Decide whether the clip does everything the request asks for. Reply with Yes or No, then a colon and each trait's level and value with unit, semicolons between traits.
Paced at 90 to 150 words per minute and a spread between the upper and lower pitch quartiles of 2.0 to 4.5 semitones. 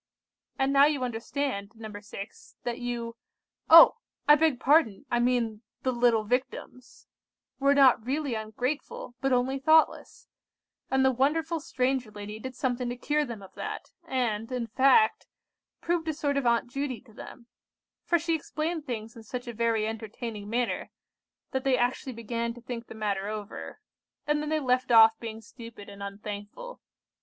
No: average, 160 wpm; average, 3.6 semitones